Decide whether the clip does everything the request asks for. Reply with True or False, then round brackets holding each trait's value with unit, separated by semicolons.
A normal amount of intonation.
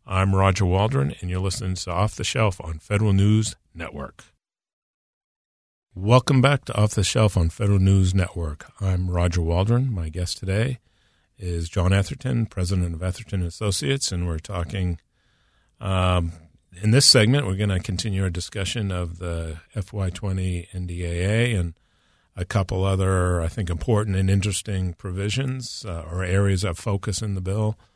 True (3.0 semitones)